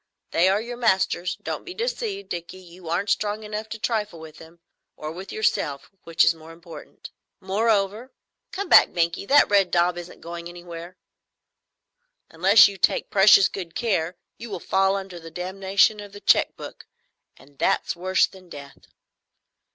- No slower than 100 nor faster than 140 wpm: No, average, 155 wpm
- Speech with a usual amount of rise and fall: Yes, average, 3.7 semitones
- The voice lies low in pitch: No, high, 190 Hz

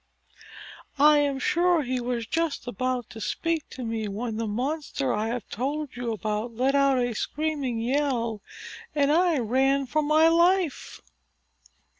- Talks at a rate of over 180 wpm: No, average, 150 wpm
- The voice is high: Yes, very high, 265 Hz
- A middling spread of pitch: Yes, average, 4.4 semitones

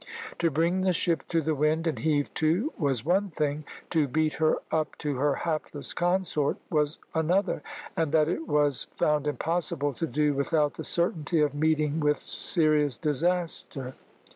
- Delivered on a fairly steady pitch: Yes, narrow, 2.1 semitones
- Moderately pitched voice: Yes, medium, 155 Hz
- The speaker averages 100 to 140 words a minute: No, average, 165 wpm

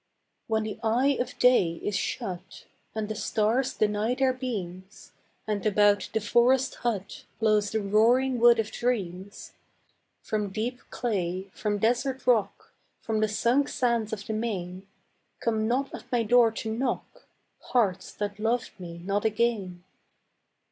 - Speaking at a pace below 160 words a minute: Yes, average, 145 wpm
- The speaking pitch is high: Yes, high, 220 Hz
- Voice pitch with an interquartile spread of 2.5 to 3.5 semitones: Yes, average, 2.9 semitones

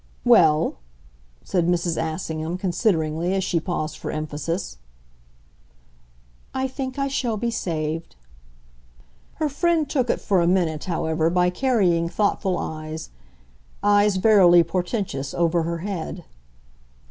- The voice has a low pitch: No, medium, 175 Hz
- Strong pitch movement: No, average, 4.4 semitones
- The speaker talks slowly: Yes, slow, 120 wpm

